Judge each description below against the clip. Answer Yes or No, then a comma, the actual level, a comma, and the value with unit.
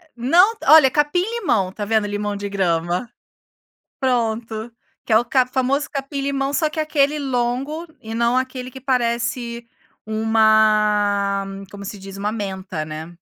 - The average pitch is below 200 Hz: No, high, 235 Hz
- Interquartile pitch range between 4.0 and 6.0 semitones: Yes, average, 4.8 semitones